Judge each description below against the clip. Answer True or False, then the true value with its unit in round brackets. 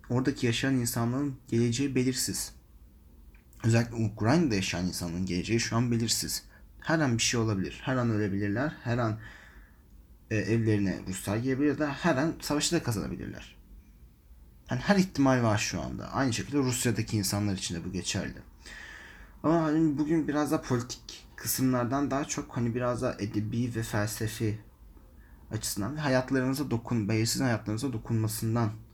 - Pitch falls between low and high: False (115 Hz)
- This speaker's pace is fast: True (145 wpm)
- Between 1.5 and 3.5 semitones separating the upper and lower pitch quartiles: False (5.0 semitones)